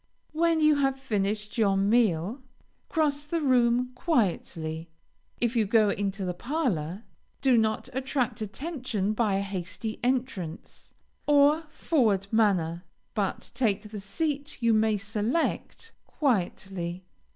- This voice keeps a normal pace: No, slow, 120 wpm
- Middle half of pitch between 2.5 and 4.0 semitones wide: No, wide, 5.5 semitones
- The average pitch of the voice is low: No, high, 220 Hz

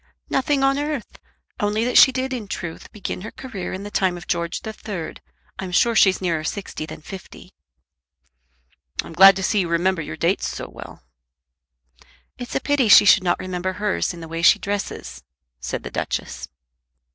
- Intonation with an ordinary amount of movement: Yes, average, 4.0 semitones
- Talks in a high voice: Yes, high, 195 Hz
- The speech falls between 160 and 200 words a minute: Yes, average, 180 wpm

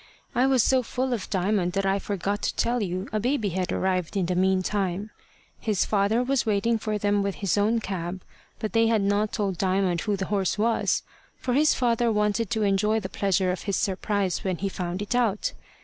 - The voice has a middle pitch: No, high, 205 Hz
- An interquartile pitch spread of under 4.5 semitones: Yes, average, 2.7 semitones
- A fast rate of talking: Yes, fast, 210 wpm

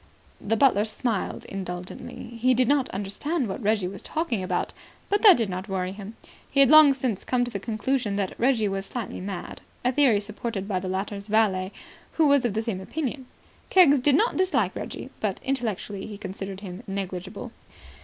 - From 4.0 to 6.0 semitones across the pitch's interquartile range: Yes, average, 5.0 semitones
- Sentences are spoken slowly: No, average, 185 wpm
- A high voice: Yes, high, 215 Hz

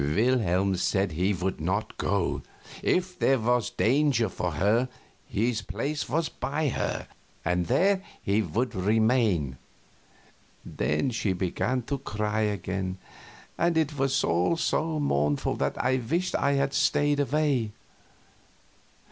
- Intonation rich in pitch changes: Yes, wide, 6.9 semitones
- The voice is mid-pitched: No, low, 115 Hz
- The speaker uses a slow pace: Yes, slow, 130 wpm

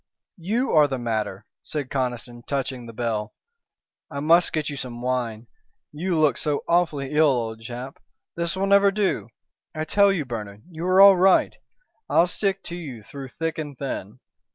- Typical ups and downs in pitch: No, wide, 6.1 semitones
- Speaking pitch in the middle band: Yes, medium, 145 Hz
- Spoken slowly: No, average, 175 wpm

